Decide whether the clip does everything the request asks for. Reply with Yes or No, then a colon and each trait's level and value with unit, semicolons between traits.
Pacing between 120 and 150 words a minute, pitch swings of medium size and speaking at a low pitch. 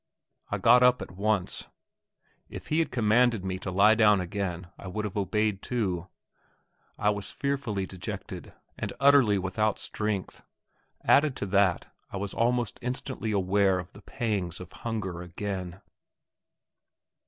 Yes: average, 140 wpm; average, 3.4 semitones; low, 100 Hz